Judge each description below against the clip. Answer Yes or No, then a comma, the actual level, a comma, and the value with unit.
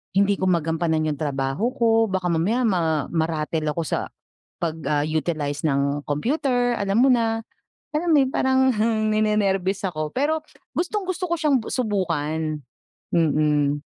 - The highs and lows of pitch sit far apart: Yes, wide, 7.2 semitones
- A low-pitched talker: No, high, 190 Hz